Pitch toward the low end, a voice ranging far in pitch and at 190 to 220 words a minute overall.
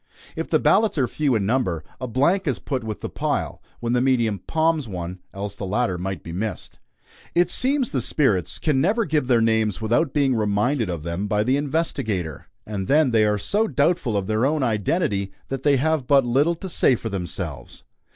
Yes: low, 120 Hz; wide, 6.4 semitones; average, 200 wpm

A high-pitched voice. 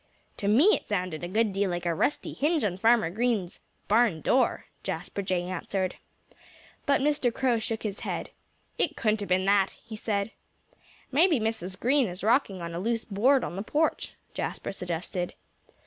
Yes: high, 205 Hz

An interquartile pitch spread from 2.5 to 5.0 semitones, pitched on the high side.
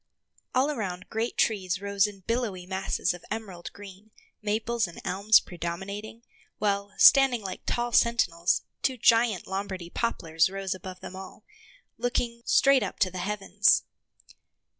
Yes: average, 3.6 semitones; high, 200 Hz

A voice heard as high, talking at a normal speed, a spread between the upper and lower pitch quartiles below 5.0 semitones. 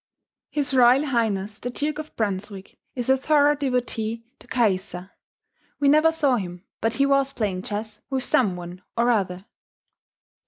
No: high, 235 Hz; average, 155 wpm; wide, 5.5 semitones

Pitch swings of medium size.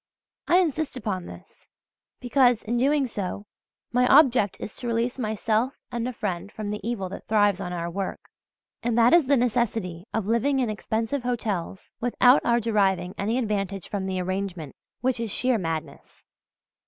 Yes: average, 3.9 semitones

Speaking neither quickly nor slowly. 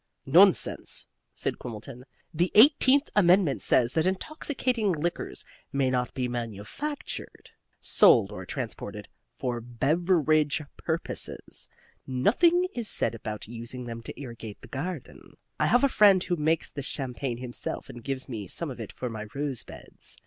Yes: average, 145 wpm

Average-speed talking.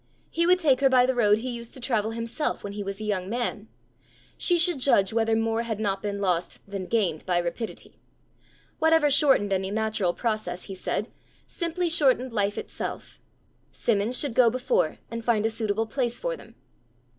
Yes: average, 185 wpm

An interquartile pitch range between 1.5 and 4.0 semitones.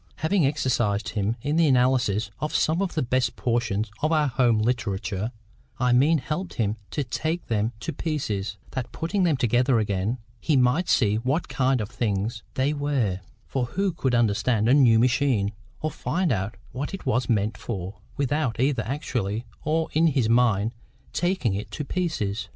No: average, 5.3 semitones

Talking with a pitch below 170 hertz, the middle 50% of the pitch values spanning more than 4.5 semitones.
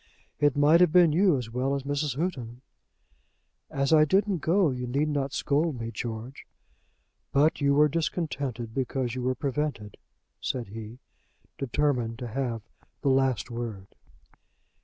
No: low, 135 Hz; average, 3.8 semitones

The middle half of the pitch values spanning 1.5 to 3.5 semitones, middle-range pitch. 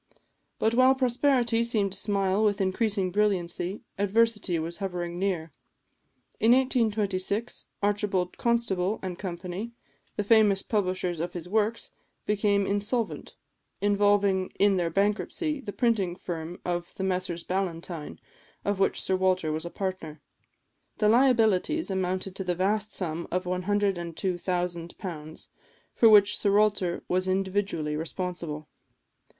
No: average, 2.9 semitones; high, 195 Hz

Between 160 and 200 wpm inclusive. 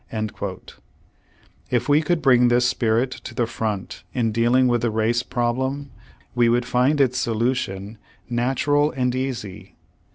No: average, 140 wpm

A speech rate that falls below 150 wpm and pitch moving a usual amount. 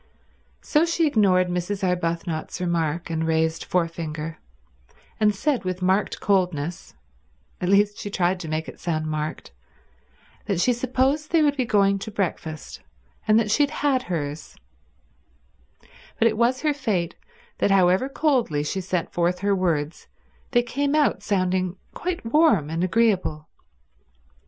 No: average, 140 wpm; wide, 5.8 semitones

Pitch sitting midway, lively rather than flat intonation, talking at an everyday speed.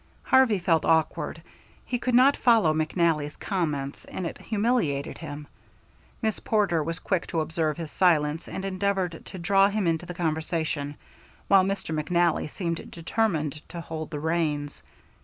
No: medium, 170 Hz; average, 3.9 semitones; average, 150 wpm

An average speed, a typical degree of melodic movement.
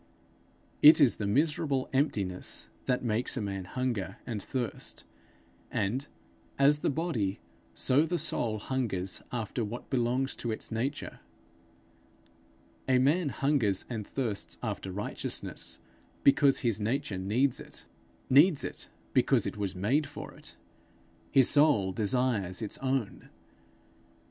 No: slow, 125 wpm; average, 5.0 semitones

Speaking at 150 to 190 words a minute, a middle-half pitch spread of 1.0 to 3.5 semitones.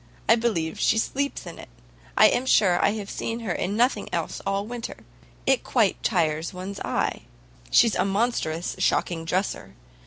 No: average, 165 wpm; average, 4.8 semitones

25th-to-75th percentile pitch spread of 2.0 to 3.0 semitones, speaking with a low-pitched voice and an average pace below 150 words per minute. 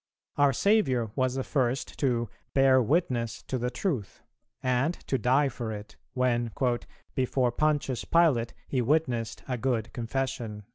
Yes: narrow, 2.5 semitones; low, 130 Hz; average, 140 wpm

